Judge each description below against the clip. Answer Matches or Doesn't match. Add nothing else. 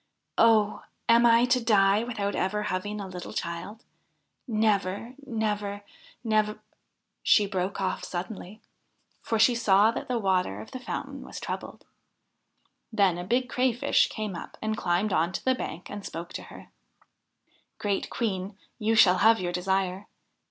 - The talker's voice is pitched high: Matches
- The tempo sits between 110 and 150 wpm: Doesn't match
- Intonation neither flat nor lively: Matches